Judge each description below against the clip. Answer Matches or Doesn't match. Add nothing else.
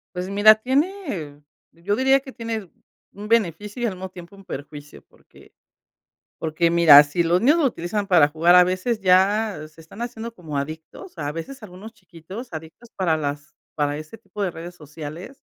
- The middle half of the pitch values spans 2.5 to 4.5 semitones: Doesn't match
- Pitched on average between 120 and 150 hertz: Doesn't match